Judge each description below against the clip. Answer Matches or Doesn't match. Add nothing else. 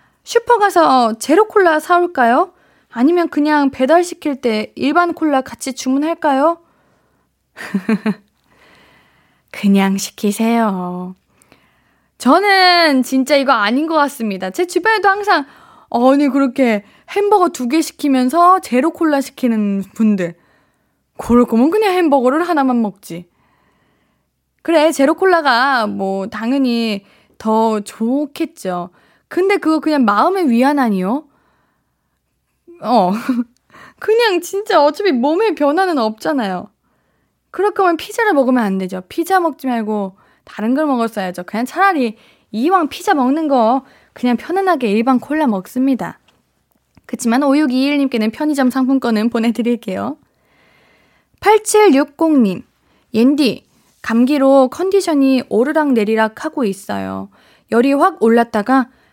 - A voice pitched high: Matches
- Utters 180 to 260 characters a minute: Matches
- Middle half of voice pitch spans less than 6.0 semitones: Doesn't match